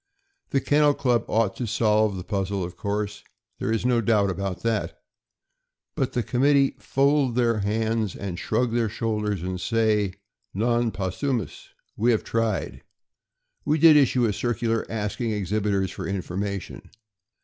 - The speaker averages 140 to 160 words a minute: Yes, average, 150 wpm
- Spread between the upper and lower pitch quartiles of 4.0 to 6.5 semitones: No, average, 3.1 semitones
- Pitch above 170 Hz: No, low, 110 Hz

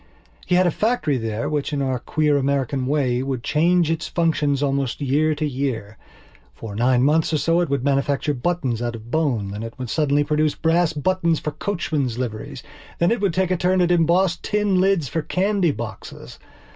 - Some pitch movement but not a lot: Yes, average, 4.7 semitones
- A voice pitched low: No, medium, 150 Hz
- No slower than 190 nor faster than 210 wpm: Yes, average, 195 wpm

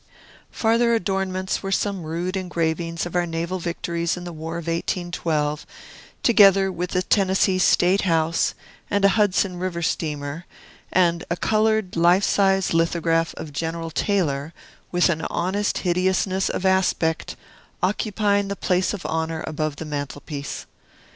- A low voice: No, medium, 175 Hz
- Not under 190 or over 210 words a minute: No, average, 140 wpm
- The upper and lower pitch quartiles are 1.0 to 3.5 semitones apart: Yes, average, 2.8 semitones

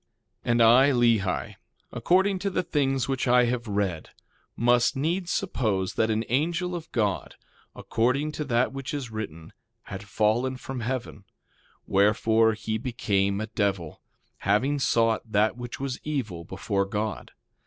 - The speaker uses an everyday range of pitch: Yes, average, 4.4 semitones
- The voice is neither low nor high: No, low, 115 Hz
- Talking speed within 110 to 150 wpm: Yes, average, 145 wpm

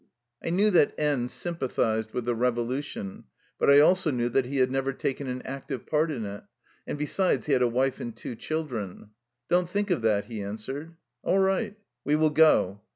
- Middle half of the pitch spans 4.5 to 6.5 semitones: Yes, average, 4.9 semitones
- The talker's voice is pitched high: No, low, 135 Hz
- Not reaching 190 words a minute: No, average, 200 wpm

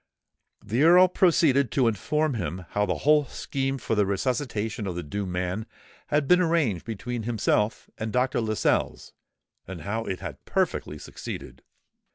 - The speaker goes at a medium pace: Yes, average, 155 wpm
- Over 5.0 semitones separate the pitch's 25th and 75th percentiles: Yes, wide, 5.5 semitones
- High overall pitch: No, low, 115 Hz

